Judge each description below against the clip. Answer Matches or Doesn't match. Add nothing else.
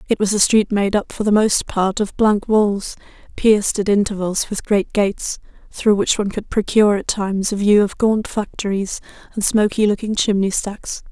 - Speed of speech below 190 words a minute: Doesn't match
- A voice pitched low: Doesn't match